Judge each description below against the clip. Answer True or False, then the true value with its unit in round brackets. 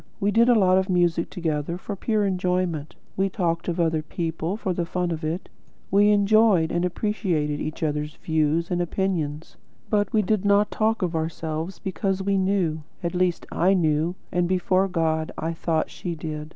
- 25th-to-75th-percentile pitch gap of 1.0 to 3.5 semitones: True (3.2 semitones)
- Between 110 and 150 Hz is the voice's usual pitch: False (175 Hz)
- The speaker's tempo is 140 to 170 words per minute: False (180 wpm)